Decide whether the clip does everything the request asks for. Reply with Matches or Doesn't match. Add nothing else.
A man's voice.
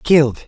Matches